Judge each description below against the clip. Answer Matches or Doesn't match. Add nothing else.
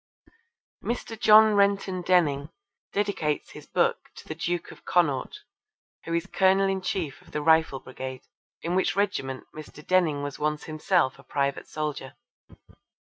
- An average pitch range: Matches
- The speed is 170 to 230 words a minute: Doesn't match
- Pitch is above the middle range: Doesn't match